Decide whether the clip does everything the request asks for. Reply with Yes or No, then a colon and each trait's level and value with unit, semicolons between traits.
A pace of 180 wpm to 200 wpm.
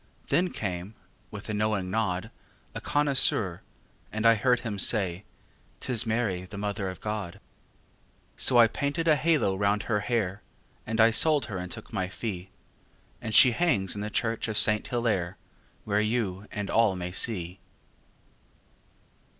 No: average, 155 wpm